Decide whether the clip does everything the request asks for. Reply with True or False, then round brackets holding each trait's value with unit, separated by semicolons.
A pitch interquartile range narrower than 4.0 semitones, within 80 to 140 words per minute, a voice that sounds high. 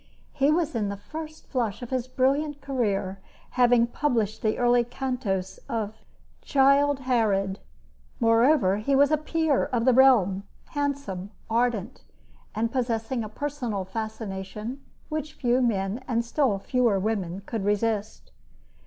False (4.5 semitones; 135 wpm; 235 Hz)